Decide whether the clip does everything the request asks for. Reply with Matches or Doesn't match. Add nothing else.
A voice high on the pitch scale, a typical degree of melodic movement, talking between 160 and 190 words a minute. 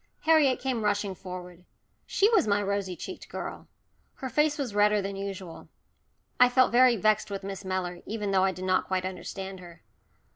Matches